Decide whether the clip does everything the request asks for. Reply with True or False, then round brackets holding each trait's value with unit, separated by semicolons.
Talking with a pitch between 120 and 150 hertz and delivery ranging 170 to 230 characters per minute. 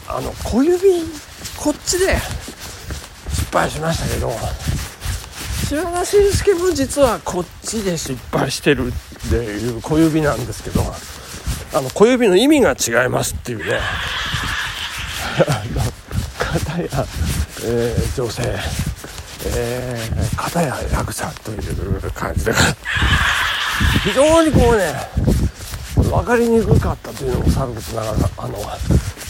True (135 Hz; 210 characters per minute)